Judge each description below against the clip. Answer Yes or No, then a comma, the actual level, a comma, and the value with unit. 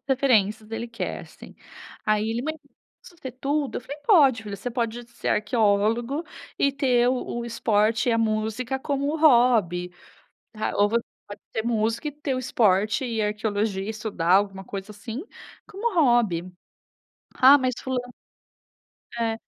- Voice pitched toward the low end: No, high, 230 Hz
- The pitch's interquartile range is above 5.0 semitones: No, average, 3.6 semitones